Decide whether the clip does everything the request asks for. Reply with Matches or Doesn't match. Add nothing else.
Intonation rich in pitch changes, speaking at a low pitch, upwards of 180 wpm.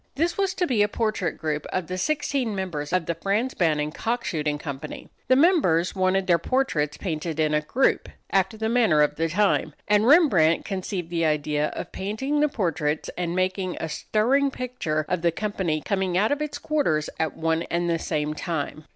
Doesn't match